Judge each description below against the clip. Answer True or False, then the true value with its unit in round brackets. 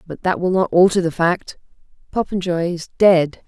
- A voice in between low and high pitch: True (175 Hz)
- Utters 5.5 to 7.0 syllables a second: False (4.7 syllables/s)